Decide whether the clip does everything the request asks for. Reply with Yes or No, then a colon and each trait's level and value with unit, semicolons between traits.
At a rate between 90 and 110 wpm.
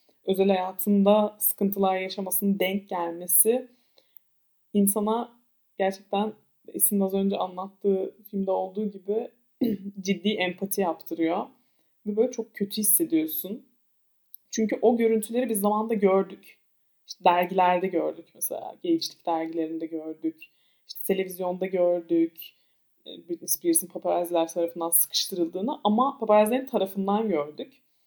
Yes: average, 105 wpm